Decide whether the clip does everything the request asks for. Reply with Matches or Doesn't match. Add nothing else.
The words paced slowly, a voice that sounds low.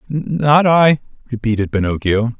Matches